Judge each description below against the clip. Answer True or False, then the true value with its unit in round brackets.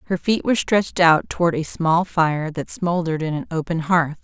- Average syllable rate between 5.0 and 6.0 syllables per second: True (5.3 syllables/s)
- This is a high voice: False (170 Hz)